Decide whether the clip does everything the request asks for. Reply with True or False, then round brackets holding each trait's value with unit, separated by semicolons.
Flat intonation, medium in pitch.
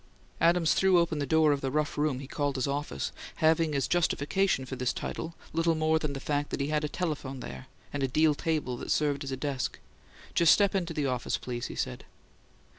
False (3.0 semitones; 150 Hz)